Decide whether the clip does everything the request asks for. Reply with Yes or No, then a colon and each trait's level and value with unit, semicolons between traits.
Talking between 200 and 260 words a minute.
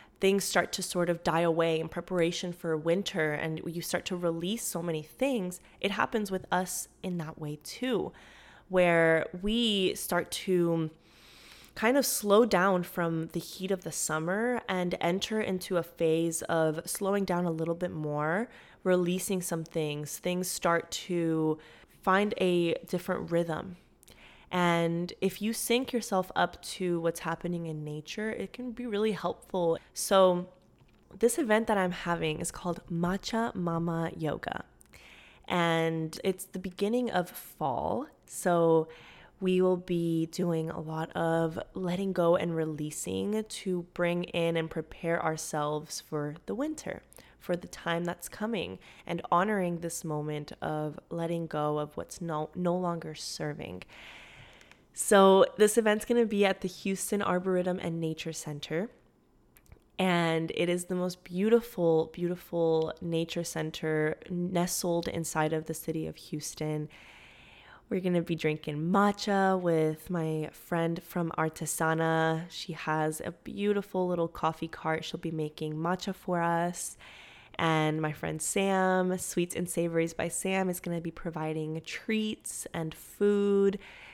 No: average, 145 wpm